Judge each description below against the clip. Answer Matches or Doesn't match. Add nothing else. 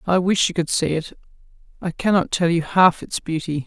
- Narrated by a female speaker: Matches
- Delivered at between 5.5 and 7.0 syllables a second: Doesn't match